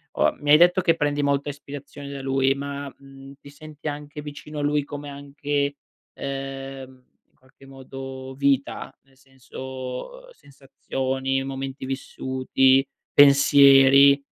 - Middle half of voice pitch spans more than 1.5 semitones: No, narrow, 1.2 semitones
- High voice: No, medium, 140 Hz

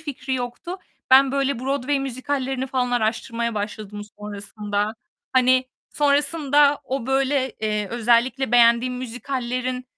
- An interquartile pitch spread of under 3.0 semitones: Yes, narrow, 2.6 semitones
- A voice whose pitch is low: No, very high, 255 Hz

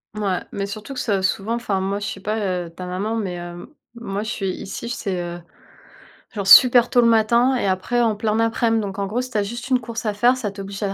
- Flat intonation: No, average, 3.1 semitones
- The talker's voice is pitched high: Yes, high, 210 Hz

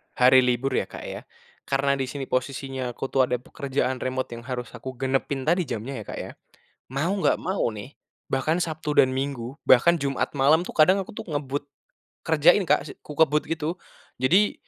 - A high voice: No, low, 135 Hz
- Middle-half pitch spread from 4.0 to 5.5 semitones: No, average, 3.1 semitones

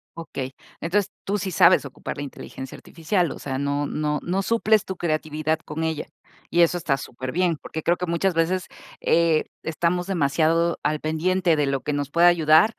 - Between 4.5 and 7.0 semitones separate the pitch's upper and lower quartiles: No, average, 3.0 semitones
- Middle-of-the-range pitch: Yes, medium, 165 Hz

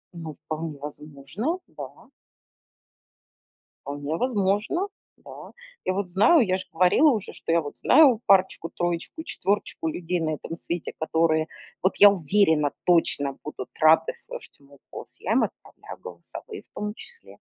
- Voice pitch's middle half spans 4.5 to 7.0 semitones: Yes, average, 4.9 semitones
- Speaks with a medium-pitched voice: Yes, medium, 175 Hz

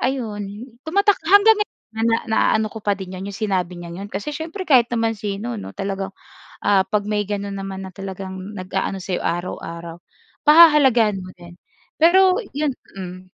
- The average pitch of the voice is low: No, high, 205 Hz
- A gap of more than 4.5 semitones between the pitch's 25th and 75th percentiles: Yes, average, 4.9 semitones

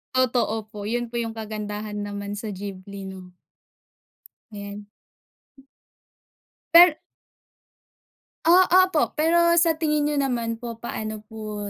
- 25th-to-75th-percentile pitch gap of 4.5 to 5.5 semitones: Yes, average, 5.1 semitones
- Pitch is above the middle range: Yes, high, 220 Hz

